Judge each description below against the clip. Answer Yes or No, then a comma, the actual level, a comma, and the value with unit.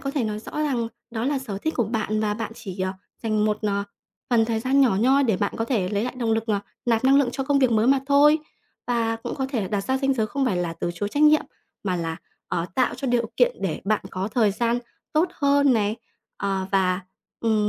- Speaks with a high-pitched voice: Yes, high, 225 Hz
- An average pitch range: Yes, average, 4.4 semitones